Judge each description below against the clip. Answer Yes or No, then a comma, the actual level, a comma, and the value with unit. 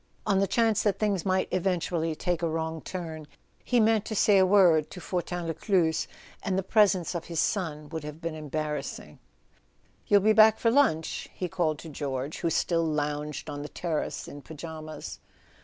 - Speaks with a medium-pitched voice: Yes, medium, 170 Hz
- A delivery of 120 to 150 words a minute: No, average, 180 wpm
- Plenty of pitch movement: No, average, 3.7 semitones